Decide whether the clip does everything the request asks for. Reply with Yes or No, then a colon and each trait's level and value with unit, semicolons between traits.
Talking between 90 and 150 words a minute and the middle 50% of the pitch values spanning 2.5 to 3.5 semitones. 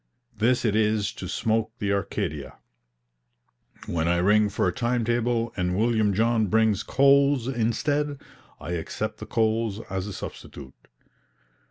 Yes: average, 140 wpm; average, 2.9 semitones